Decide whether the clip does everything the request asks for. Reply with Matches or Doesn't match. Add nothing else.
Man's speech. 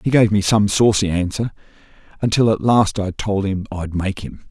Matches